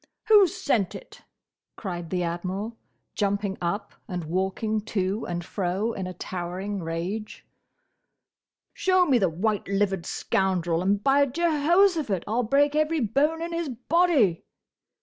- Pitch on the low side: No, high, 205 Hz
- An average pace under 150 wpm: Yes, slow, 135 wpm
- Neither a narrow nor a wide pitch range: No, wide, 7.6 semitones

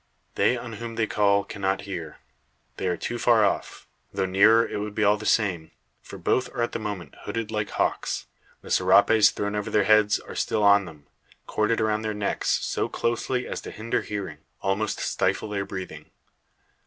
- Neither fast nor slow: Yes, average, 190 wpm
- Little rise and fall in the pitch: Yes, narrow, 1.8 semitones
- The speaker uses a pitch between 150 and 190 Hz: No, low, 105 Hz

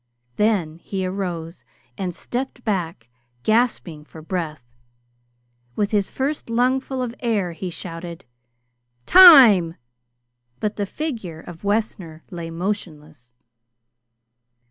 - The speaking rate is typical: No, slow, 100 wpm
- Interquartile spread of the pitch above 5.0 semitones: Yes, wide, 5.4 semitones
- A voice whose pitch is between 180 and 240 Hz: Yes, high, 190 Hz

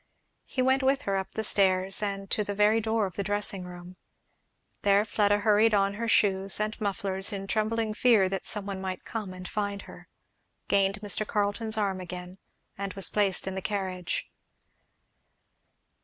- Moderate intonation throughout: No, narrow, 1.8 semitones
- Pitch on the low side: No, high, 200 Hz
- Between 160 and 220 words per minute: Yes, average, 170 wpm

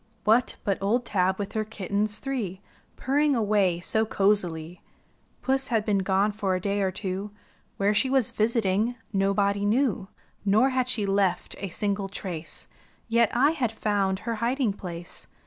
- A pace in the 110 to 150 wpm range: No, average, 160 wpm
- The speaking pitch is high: Yes, high, 205 Hz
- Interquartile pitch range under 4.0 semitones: Yes, average, 3.0 semitones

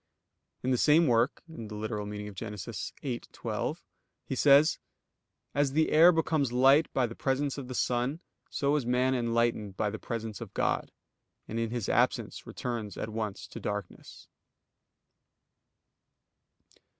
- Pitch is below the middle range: Yes, low, 120 Hz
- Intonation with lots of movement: No, average, 4.3 semitones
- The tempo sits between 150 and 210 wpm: No, average, 140 wpm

